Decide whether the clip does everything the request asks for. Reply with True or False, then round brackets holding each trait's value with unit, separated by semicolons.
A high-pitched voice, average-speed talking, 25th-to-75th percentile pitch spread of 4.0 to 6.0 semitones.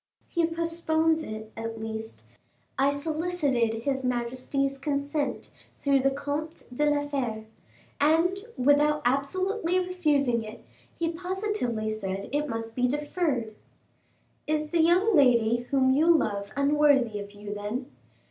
False (280 Hz; 130 wpm; 5.4 semitones)